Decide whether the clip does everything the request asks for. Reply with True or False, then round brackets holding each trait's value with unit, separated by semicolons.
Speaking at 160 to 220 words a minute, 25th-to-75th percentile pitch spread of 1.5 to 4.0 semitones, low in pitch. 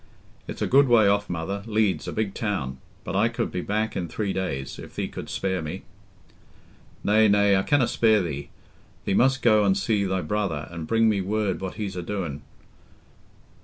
True (190 wpm; 2.9 semitones; 100 Hz)